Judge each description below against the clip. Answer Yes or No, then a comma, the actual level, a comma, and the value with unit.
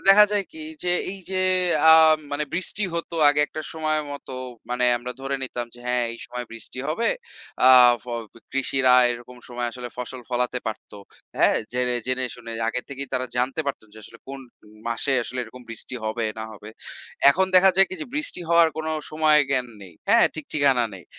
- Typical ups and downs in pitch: Yes, average, 4.2 semitones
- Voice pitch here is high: No, low, 130 Hz